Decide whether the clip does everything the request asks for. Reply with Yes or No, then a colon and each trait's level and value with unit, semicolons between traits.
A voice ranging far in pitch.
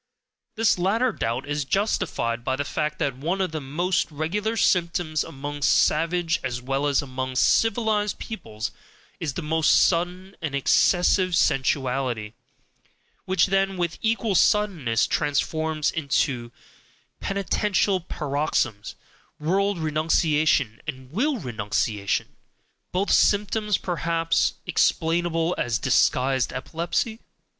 Yes: wide, 5.7 semitones